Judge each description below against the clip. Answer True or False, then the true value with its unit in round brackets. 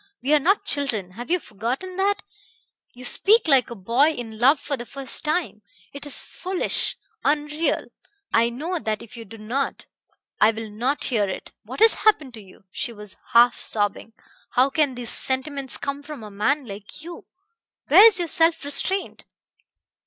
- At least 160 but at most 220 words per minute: True (175 wpm)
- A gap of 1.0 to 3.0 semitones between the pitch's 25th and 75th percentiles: False (5.3 semitones)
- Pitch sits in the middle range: False (270 Hz)